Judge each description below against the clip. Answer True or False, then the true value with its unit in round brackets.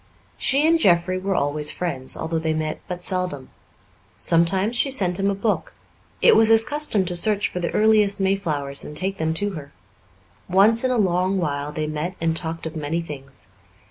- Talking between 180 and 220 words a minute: True (190 wpm)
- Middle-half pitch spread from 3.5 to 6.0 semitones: True (4.2 semitones)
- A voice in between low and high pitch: True (180 Hz)